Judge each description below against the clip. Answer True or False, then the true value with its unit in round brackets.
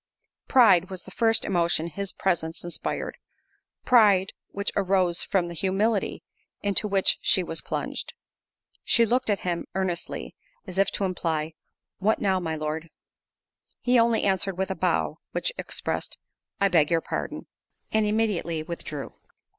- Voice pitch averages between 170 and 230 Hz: True (190 Hz)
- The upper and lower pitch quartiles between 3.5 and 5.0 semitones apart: False (3.1 semitones)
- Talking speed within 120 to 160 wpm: True (140 wpm)